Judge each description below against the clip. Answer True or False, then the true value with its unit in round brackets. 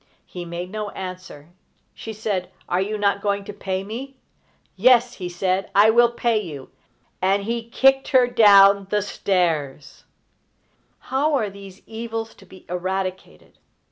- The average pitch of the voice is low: False (200 Hz)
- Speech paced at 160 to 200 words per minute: False (145 wpm)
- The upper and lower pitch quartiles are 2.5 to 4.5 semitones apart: True (3.4 semitones)